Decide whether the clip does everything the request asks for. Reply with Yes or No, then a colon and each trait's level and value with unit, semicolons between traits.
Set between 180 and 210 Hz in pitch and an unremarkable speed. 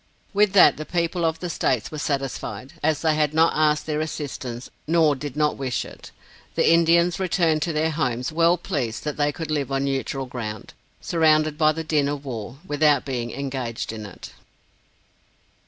No: medium, 150 Hz; average, 180 wpm